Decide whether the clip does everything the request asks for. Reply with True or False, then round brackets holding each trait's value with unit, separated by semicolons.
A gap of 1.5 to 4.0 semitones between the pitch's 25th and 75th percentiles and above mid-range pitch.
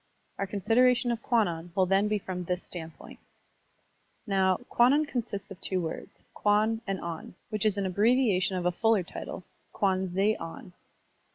True (3.3 semitones; 195 Hz)